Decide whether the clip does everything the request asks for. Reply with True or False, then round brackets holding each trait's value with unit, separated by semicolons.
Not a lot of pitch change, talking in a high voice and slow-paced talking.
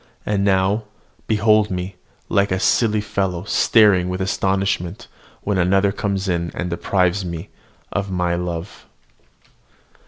False (2.2 semitones; 95 Hz; 125 wpm)